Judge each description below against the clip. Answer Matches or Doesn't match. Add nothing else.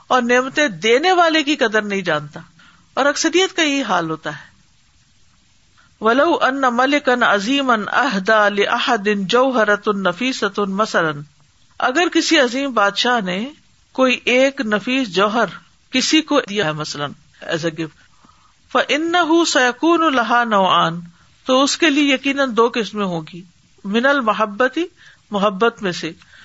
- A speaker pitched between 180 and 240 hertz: Matches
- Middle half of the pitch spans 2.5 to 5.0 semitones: Doesn't match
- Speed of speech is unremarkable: Doesn't match